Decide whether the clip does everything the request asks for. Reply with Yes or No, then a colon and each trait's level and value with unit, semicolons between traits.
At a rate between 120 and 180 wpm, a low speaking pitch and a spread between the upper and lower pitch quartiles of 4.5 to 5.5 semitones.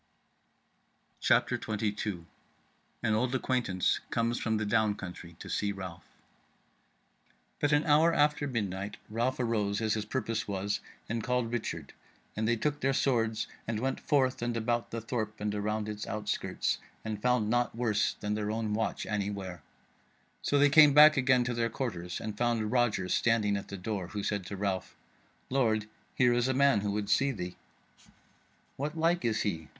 No: average, 170 wpm; low, 110 Hz; average, 3.2 semitones